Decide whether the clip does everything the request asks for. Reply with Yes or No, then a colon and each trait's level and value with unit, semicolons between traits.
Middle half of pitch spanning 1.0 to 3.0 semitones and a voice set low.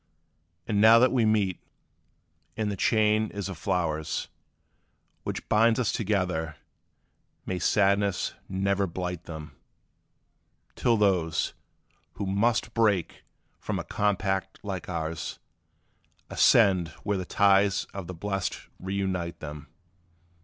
Yes: average, 2.7 semitones; very low, 95 Hz